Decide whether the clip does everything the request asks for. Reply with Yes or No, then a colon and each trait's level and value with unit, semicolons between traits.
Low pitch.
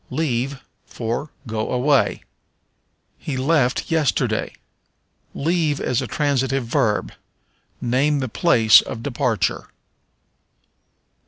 Yes: low, 130 Hz